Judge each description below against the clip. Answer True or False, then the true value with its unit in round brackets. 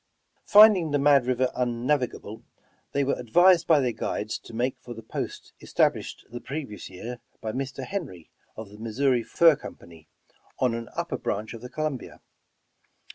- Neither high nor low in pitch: False (125 Hz)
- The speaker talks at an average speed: True (165 wpm)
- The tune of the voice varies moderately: True (4.2 semitones)